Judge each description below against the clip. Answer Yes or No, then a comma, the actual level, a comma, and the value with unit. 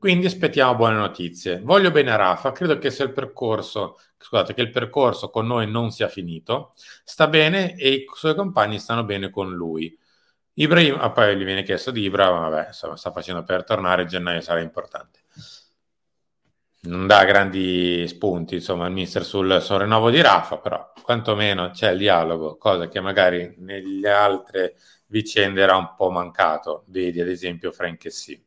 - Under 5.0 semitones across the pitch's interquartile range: No, wide, 5.6 semitones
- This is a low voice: Yes, low, 100 Hz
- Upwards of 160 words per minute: Yes, fast, 170 wpm